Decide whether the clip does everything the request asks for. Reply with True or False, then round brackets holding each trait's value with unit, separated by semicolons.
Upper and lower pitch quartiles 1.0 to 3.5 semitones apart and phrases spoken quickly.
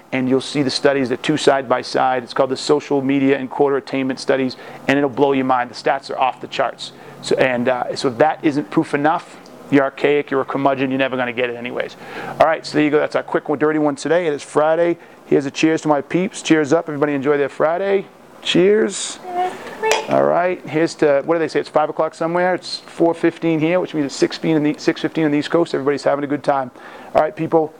True (2.9 semitones; 245 wpm)